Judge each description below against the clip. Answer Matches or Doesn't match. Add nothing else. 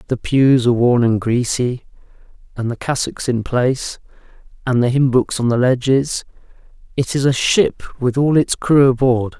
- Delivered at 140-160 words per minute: Doesn't match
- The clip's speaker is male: Matches